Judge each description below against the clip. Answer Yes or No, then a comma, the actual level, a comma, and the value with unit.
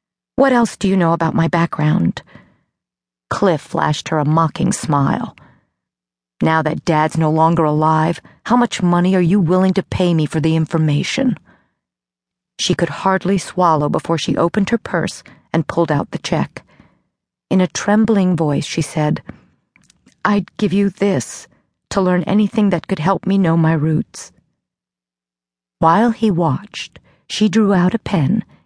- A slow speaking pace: No, average, 155 wpm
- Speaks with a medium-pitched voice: Yes, medium, 170 Hz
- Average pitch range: Yes, average, 4.0 semitones